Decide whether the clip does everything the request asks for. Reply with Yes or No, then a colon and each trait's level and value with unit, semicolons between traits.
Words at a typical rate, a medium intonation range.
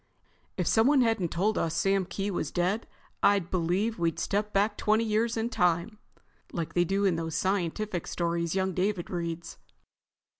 Yes: average, 160 wpm; average, 3.8 semitones